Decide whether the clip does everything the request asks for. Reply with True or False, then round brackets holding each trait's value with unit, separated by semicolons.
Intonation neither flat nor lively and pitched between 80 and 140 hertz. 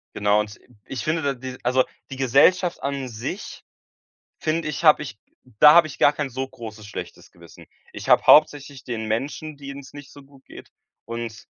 True (4.0 semitones; 135 Hz)